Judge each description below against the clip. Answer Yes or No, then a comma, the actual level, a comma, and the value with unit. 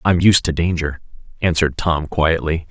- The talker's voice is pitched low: Yes, very low, 80 Hz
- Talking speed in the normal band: Yes, average, 155 wpm